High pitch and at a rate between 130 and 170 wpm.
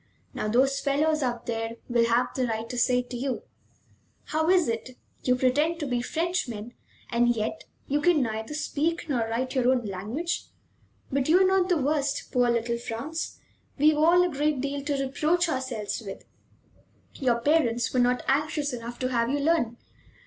No: very high, 260 Hz; average, 180 wpm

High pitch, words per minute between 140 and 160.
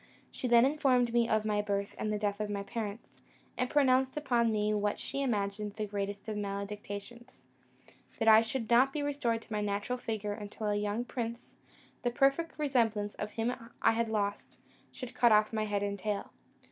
No: high, 220 Hz; average, 190 wpm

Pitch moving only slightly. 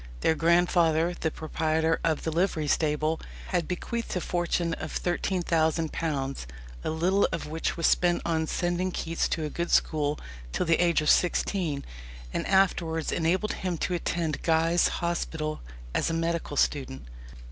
Yes: narrow, 1.8 semitones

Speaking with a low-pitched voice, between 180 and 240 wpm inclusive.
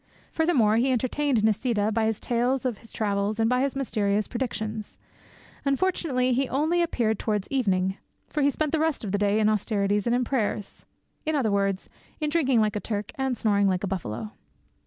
No: high, 225 Hz; average, 185 wpm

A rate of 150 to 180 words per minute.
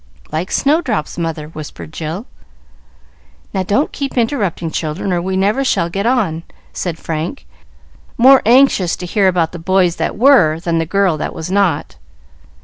Yes: average, 155 wpm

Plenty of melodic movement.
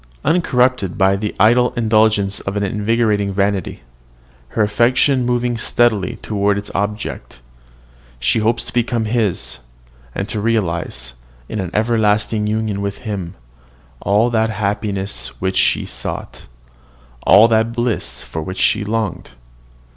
No: narrow, 2.5 semitones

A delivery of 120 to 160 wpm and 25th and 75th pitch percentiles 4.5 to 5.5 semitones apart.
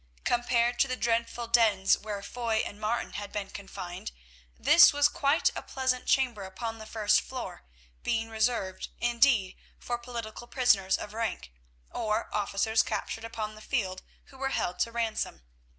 No: average, 155 wpm; narrow, 2.6 semitones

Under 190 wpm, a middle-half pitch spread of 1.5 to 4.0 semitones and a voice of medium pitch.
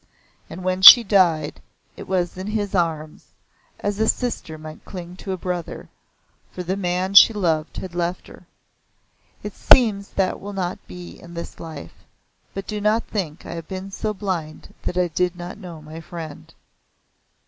Yes: average, 170 wpm; average, 2.8 semitones; medium, 180 Hz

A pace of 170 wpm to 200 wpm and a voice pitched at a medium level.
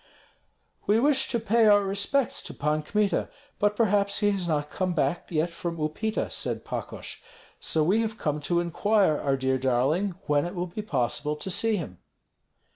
Yes: average, 180 wpm; medium, 180 Hz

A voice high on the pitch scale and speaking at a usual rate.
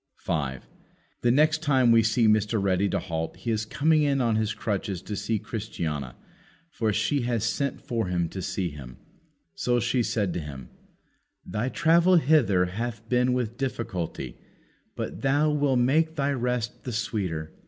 No: low, 115 Hz; average, 165 wpm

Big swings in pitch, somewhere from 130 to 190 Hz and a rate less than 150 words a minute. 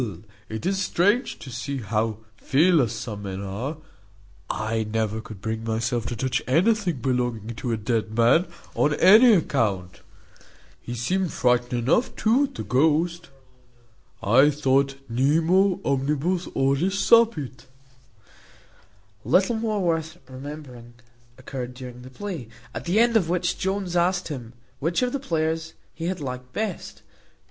Yes: wide, 7.0 semitones; medium, 140 Hz; average, 140 wpm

